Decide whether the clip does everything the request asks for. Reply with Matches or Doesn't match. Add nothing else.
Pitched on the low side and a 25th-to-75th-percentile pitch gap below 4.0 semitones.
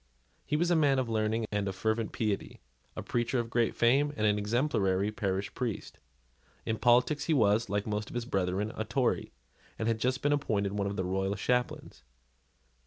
Matches